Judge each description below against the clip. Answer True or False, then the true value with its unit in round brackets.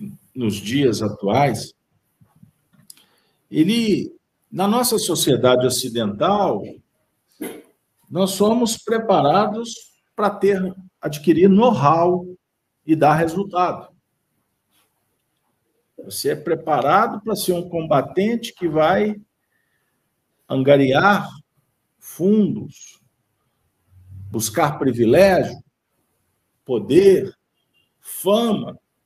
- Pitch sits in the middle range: True (180 Hz)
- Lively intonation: True (7.2 semitones)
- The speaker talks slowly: True (70 wpm)